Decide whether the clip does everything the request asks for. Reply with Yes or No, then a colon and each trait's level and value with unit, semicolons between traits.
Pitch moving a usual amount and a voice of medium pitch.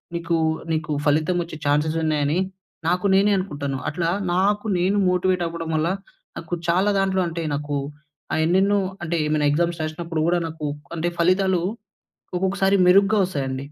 Yes: average, 3.1 semitones; medium, 170 Hz